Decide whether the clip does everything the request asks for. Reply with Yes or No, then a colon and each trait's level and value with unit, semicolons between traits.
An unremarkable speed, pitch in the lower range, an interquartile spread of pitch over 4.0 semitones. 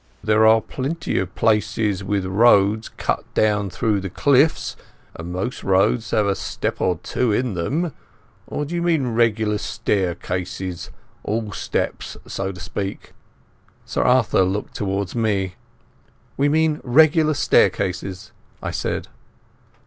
No: slow, 130 wpm; low, 105 Hz; average, 4.6 semitones